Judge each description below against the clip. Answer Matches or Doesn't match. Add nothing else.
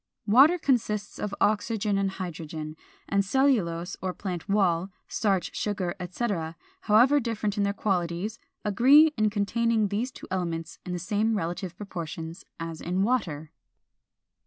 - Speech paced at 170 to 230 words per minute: Doesn't match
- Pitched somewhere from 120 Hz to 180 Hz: Doesn't match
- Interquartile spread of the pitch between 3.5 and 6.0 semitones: Matches